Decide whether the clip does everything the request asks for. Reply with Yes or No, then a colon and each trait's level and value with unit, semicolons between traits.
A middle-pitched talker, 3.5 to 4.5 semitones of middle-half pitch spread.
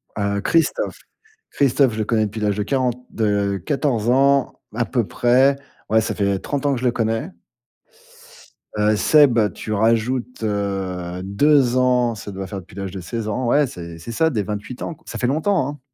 No: low, 115 Hz; average, 4.2 semitones